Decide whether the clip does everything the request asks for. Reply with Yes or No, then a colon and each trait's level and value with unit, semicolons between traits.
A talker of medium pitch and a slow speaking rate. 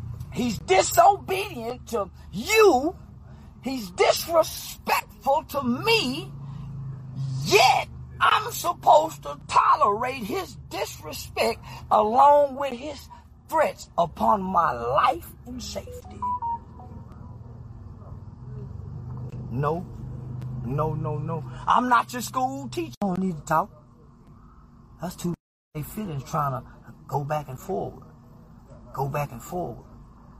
Yes: medium, 150 Hz; slow, 105 wpm